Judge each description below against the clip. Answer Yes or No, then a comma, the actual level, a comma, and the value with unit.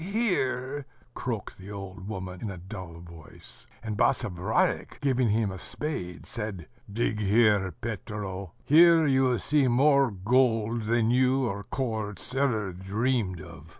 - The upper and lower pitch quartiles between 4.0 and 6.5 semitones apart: Yes, average, 5.1 semitones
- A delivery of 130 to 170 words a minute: Yes, average, 140 wpm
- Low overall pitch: Yes, low, 110 Hz